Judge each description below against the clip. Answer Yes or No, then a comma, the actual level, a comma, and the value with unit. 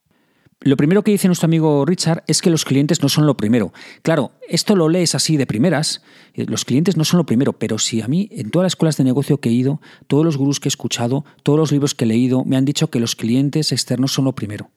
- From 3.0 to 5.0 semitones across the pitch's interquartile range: Yes, average, 3.7 semitones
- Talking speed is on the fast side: Yes, fast, 260 wpm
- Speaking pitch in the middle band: Yes, medium, 145 Hz